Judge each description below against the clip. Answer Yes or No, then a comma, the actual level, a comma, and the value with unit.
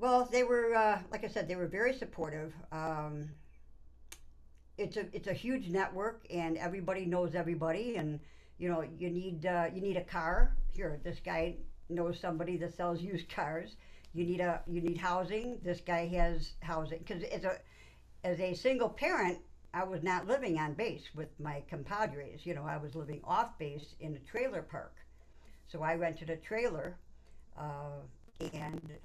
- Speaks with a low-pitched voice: No, medium, 170 Hz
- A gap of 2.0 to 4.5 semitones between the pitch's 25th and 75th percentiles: Yes, average, 3.4 semitones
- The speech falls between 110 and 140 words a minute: No, average, 175 wpm